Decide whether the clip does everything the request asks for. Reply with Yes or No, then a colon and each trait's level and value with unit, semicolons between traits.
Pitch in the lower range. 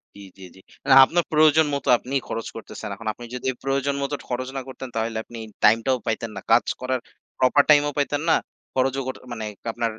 Yes: low, 130 Hz